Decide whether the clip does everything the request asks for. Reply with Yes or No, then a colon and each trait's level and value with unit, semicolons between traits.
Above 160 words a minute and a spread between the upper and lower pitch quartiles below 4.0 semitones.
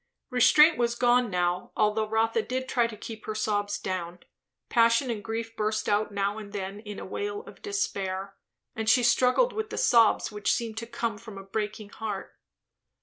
Yes: average, 185 wpm; average, 2.7 semitones